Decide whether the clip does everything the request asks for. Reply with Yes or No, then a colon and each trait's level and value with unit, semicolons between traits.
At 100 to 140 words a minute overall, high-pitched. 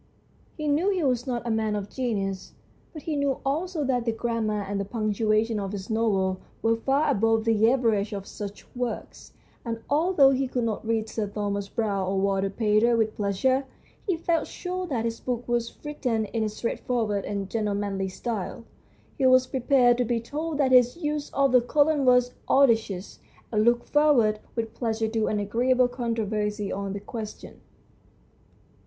No: average, 175 wpm; high, 230 Hz